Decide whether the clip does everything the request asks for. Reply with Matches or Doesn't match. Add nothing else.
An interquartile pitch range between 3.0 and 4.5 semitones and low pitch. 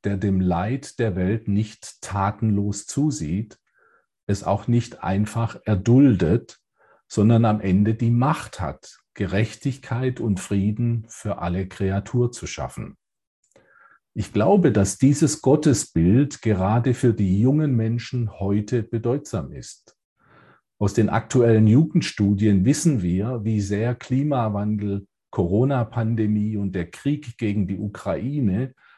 Matches